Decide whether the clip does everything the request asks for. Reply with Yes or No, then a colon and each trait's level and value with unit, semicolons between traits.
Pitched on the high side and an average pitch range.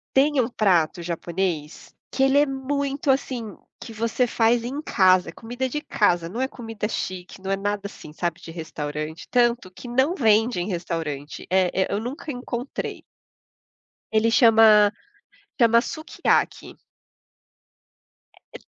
No: high, 220 Hz; wide, 5.7 semitones